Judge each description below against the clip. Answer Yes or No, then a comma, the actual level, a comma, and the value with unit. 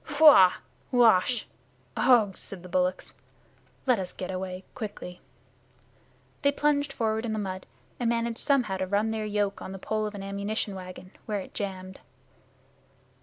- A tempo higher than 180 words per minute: No, average, 155 wpm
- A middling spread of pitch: Yes, average, 3.7 semitones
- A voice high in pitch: Yes, high, 205 Hz